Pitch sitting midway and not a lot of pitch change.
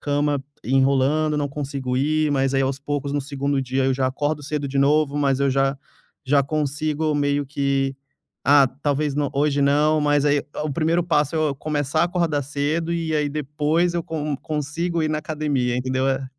Yes: medium, 145 Hz; narrow, 1.9 semitones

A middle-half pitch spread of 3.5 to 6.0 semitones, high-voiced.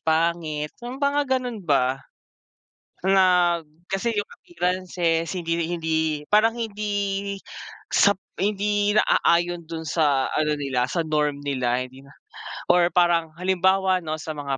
No: average, 4.3 semitones; medium, 175 Hz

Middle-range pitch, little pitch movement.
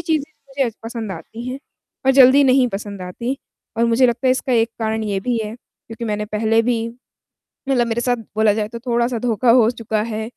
No: high, 230 Hz; narrow, 2.3 semitones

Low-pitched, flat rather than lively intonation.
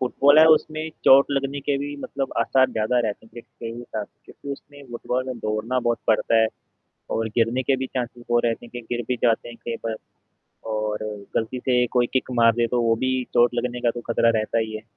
Yes: low, 120 Hz; narrow, 2.3 semitones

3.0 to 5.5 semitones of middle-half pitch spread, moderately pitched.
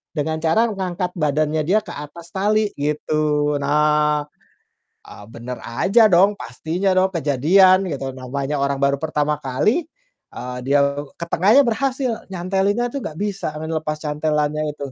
Yes: average, 4.7 semitones; medium, 155 Hz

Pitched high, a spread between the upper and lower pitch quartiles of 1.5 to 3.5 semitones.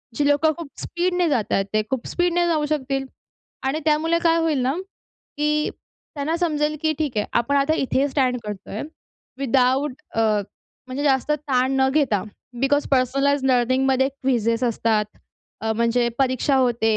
Yes: very high, 270 Hz; average, 3.2 semitones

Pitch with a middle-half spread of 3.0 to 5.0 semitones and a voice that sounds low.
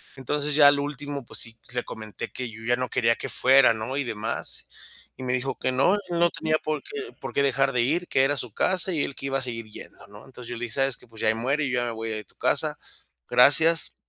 Yes: average, 3.7 semitones; low, 130 Hz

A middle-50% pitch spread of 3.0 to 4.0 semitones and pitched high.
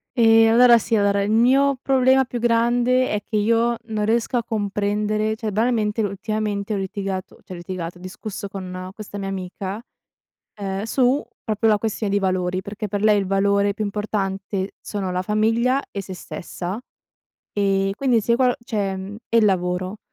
No: narrow, 2.6 semitones; high, 210 Hz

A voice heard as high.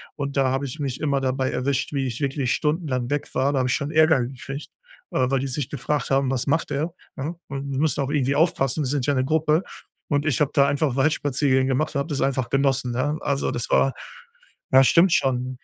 No: medium, 140 Hz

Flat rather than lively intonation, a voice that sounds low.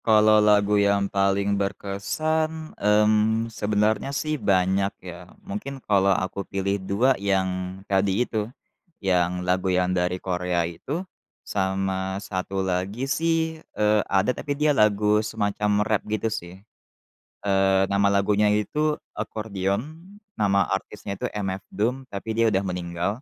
Yes: narrow, 2.3 semitones; low, 100 Hz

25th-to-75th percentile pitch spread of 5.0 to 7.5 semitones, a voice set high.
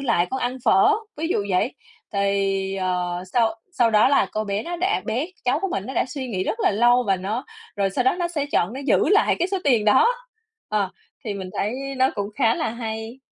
Yes: wide, 5.5 semitones; high, 230 Hz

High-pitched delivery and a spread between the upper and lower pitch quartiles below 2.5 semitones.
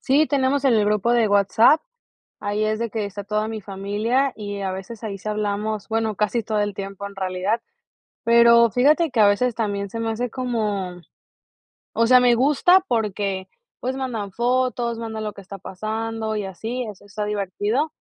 No: high, 215 Hz; average, 2.8 semitones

